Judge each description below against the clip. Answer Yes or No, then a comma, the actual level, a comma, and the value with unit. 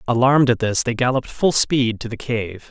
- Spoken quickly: Yes, fast, 220 wpm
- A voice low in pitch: Yes, low, 120 Hz